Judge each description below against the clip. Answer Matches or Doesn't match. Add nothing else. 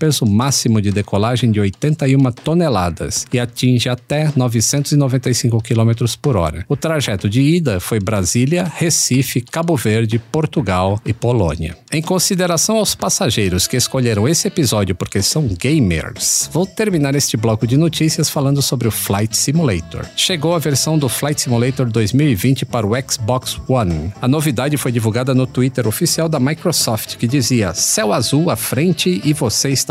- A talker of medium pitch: Doesn't match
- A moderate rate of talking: Matches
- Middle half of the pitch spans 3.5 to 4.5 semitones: Doesn't match